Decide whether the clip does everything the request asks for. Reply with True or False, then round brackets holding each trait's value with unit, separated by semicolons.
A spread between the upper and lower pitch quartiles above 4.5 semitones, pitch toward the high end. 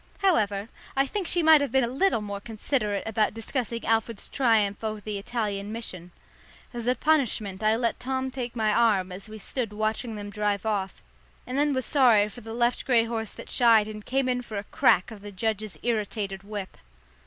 False (3.1 semitones; 225 Hz)